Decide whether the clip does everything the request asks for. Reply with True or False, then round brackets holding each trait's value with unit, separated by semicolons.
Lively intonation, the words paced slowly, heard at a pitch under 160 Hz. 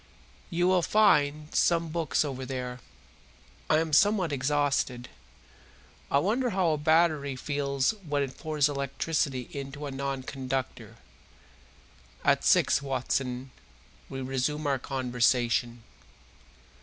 False (3.0 semitones; 115 wpm; 140 Hz)